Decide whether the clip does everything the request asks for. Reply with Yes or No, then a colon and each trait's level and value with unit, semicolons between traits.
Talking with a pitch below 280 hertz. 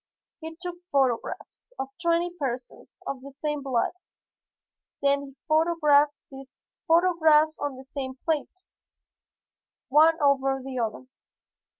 No: very high, 285 Hz